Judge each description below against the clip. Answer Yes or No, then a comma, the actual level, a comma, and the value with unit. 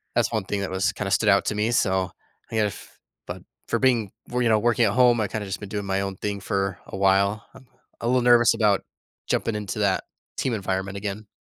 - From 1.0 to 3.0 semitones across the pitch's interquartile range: Yes, average, 2.7 semitones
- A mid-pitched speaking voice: No, low, 105 Hz